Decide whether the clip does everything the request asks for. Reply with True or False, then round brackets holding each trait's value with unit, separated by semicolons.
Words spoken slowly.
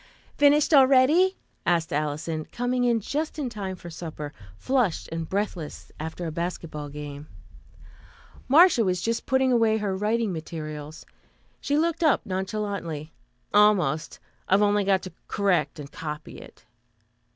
True (130 wpm)